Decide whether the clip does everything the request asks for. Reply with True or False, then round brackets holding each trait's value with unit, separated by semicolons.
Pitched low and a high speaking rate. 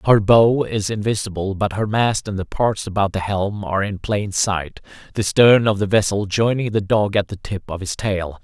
True (100 Hz; 220 wpm)